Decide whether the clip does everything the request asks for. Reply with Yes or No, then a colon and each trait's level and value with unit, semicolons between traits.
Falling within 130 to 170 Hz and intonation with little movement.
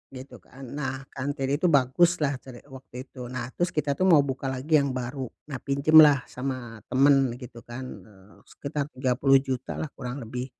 Yes: low, 135 Hz; narrow, 2.0 semitones